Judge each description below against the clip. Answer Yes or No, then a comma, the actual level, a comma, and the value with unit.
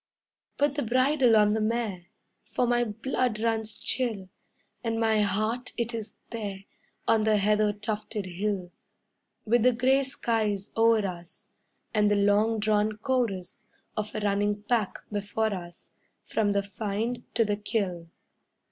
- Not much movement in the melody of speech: Yes, narrow, 2.1 semitones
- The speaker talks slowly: No, average, 145 wpm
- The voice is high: Yes, high, 215 Hz